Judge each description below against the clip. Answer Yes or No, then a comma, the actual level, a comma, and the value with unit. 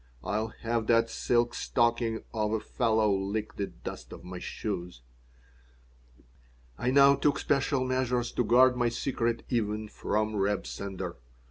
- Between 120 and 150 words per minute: Yes, average, 140 wpm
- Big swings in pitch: No, average, 2.7 semitones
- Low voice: Yes, low, 115 Hz